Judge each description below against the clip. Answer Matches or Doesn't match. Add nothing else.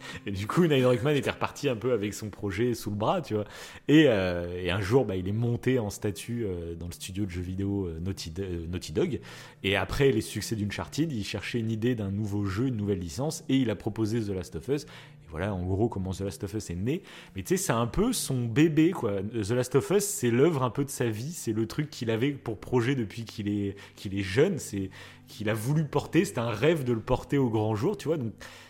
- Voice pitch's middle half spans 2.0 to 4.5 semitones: Doesn't match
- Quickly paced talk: Matches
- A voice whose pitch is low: Matches